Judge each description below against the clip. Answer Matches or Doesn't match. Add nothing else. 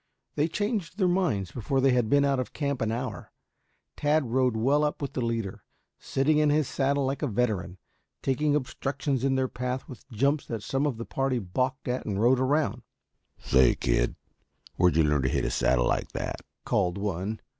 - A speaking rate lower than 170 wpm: Doesn't match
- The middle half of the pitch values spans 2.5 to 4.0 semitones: Doesn't match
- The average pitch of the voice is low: Matches